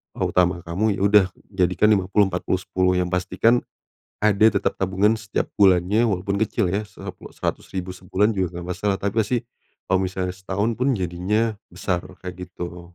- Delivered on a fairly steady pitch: Yes, narrow, 2.3 semitones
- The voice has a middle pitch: No, very low, 95 Hz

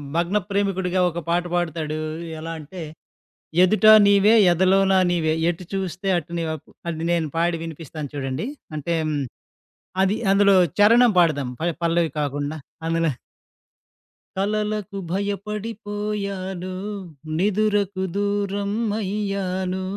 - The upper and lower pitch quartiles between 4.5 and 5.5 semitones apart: No, average, 3.3 semitones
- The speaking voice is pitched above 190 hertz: No, medium, 185 Hz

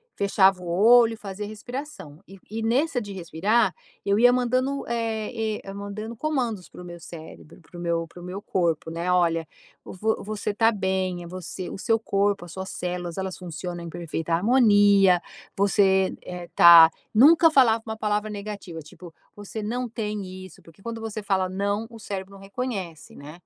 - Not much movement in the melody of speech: No, average, 3.8 semitones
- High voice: Yes, high, 200 Hz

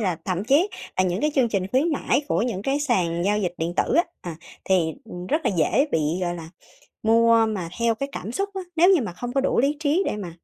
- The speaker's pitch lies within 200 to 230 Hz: Yes, high, 220 Hz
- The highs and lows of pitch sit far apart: Yes, wide, 7.6 semitones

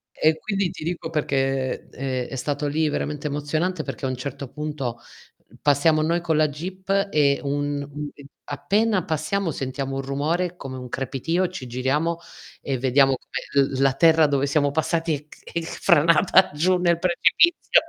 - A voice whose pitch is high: No, medium, 150 Hz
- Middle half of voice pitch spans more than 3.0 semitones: Yes, average, 3.5 semitones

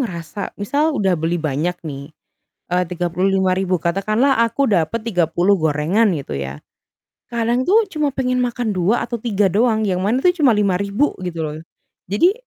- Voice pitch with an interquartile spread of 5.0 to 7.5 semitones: Yes, average, 5.3 semitones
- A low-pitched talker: No, high, 200 Hz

